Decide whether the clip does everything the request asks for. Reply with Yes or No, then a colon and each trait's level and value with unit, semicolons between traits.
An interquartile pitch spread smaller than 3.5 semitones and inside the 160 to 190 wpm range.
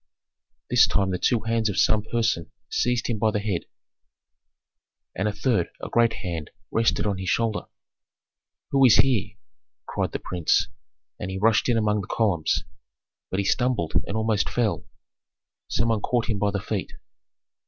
Yes: average, 2.9 semitones; average, 165 wpm